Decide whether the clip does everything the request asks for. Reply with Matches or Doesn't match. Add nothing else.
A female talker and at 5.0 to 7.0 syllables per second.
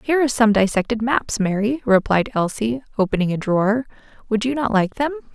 Matches